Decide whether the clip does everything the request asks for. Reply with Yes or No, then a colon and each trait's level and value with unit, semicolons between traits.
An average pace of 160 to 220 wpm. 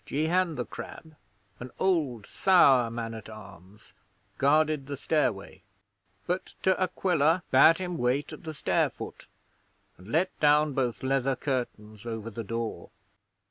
No: average, 140 wpm